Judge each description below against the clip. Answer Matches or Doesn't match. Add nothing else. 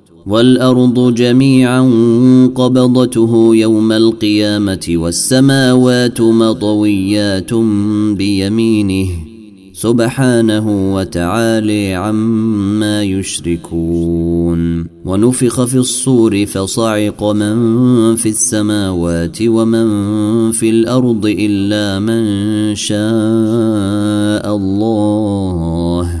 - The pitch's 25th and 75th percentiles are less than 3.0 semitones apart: Matches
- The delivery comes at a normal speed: Doesn't match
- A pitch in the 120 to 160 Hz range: Doesn't match